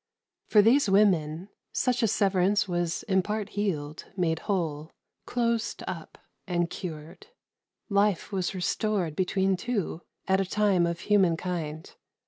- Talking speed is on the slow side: Yes, slow, 130 wpm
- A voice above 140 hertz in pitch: Yes, high, 190 Hz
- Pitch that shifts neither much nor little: Yes, average, 3.5 semitones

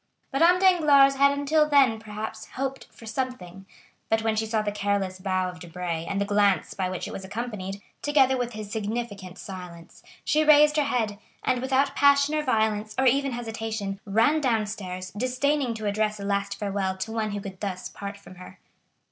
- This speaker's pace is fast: No, average, 185 wpm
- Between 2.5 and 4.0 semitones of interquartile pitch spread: No, average, 5.0 semitones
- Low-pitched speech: No, high, 220 Hz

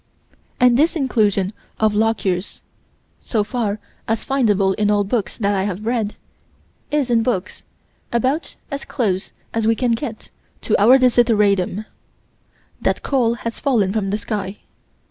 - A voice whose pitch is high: Yes, high, 220 Hz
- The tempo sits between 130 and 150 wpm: Yes, average, 145 wpm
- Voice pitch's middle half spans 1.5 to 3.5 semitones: Yes, average, 3.2 semitones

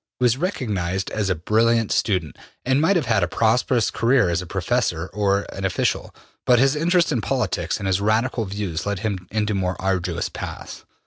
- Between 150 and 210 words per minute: Yes, average, 190 wpm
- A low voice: Yes, low, 105 Hz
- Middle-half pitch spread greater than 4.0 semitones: Yes, average, 4.7 semitones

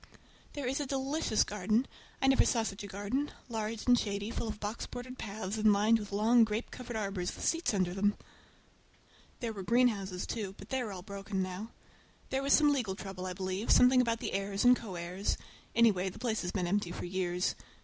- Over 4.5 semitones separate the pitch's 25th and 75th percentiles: No, average, 4.0 semitones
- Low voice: No, high, 210 Hz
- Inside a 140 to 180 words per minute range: No, fast, 205 wpm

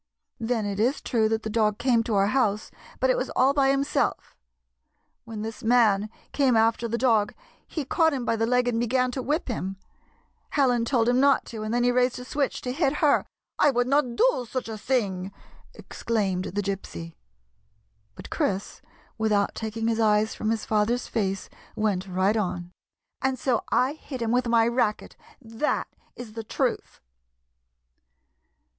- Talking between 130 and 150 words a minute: No, average, 185 wpm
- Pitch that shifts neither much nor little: Yes, average, 3.0 semitones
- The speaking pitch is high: Yes, high, 230 Hz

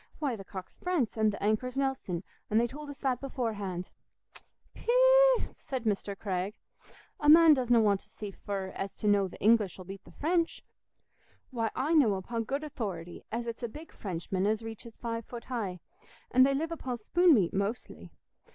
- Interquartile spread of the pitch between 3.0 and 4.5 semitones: No, wide, 5.4 semitones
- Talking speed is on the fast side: No, average, 185 wpm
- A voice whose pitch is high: Yes, high, 230 Hz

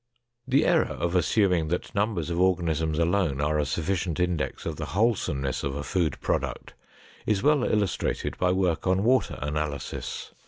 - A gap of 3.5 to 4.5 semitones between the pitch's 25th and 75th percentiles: Yes, average, 4.0 semitones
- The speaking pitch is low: Yes, very low, 90 Hz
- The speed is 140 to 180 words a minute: Yes, average, 160 wpm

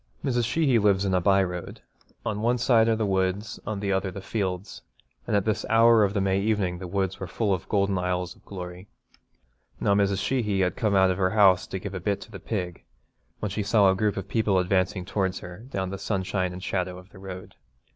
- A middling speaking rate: No, fast, 230 wpm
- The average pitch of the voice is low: Yes, low, 100 Hz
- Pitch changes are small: Yes, narrow, 2.3 semitones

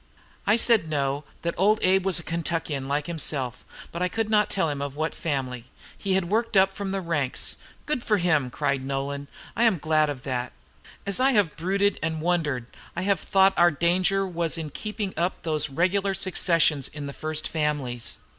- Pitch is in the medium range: Yes, medium, 170 Hz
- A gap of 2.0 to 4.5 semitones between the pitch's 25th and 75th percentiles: No, average, 4.9 semitones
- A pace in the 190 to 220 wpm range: Yes, average, 195 wpm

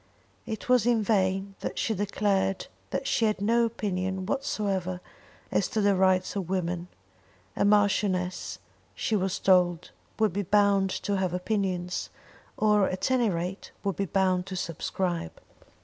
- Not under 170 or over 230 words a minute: No, average, 150 wpm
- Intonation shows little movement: Yes, narrow, 2.2 semitones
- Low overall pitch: No, high, 195 Hz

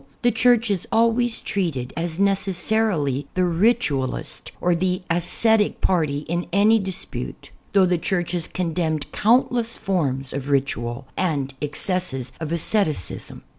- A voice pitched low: No, medium, 180 Hz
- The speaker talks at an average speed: No, slow, 130 wpm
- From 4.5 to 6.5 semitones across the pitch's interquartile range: Yes, wide, 5.5 semitones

